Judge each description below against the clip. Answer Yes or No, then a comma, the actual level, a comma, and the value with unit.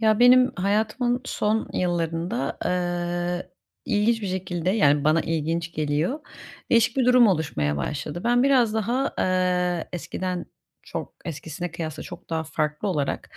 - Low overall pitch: No, medium, 180 Hz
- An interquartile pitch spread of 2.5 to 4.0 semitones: No, average, 5.1 semitones